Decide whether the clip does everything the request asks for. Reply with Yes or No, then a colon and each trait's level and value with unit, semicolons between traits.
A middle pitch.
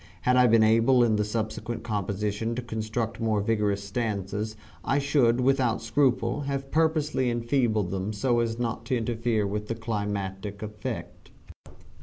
No: low, 115 Hz